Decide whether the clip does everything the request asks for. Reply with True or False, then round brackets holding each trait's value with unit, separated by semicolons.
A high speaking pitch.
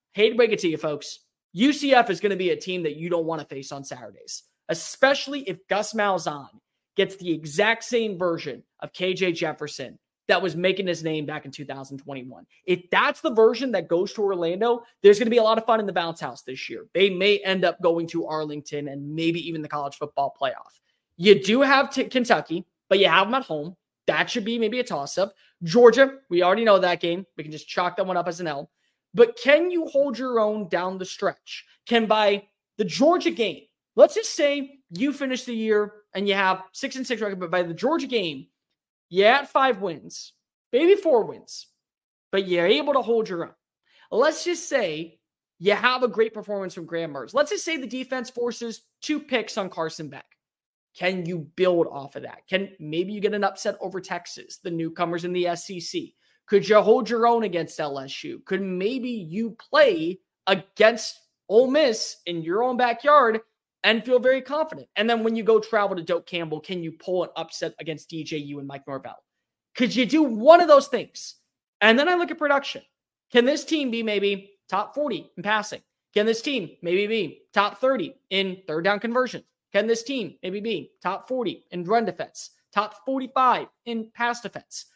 True (200 Hz)